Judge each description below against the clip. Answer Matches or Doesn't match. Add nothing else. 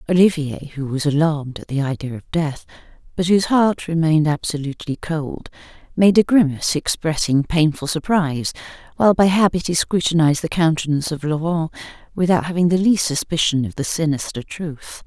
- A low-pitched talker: Doesn't match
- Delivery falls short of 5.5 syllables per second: Doesn't match